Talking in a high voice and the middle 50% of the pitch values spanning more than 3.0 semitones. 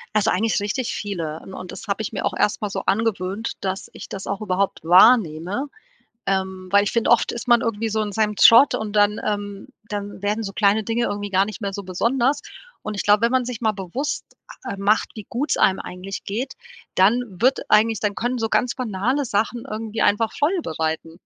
No: high, 210 Hz; average, 2.7 semitones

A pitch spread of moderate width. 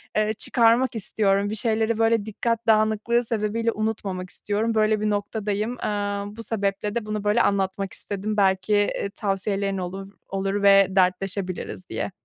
No: narrow, 1.8 semitones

